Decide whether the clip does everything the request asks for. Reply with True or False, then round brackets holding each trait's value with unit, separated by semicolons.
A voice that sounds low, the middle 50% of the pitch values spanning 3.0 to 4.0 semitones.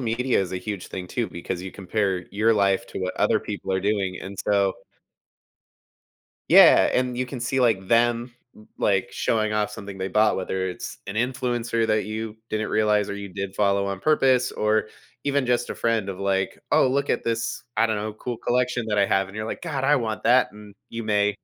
True (110 Hz; 3.3 semitones)